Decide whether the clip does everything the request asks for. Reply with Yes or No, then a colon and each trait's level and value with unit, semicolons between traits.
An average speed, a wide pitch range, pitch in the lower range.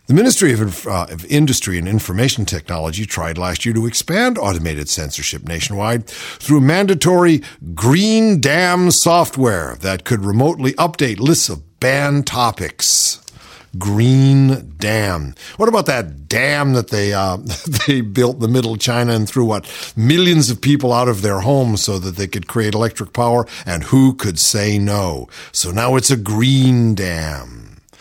Yes: average, 160 wpm; wide, 5.9 semitones; low, 115 Hz